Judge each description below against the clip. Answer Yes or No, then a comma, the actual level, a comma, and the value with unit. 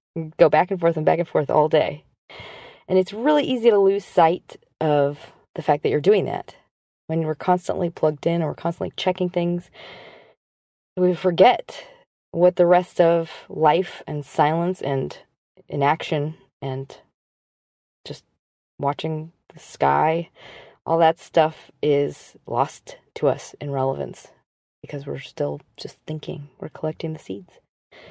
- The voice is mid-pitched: Yes, medium, 160 Hz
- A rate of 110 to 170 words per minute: Yes, average, 145 wpm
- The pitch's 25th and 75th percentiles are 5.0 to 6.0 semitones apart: No, average, 3.7 semitones